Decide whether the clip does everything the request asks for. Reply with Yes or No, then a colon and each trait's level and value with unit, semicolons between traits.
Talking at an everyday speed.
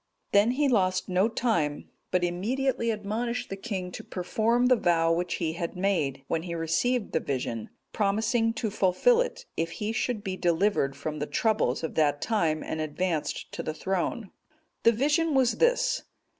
Yes: average, 170 wpm